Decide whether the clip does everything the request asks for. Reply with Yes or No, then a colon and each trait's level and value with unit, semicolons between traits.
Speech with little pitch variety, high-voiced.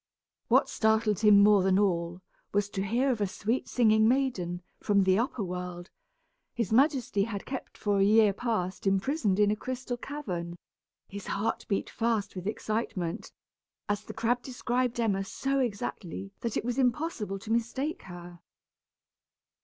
No: average, 3.8 semitones; high, 210 Hz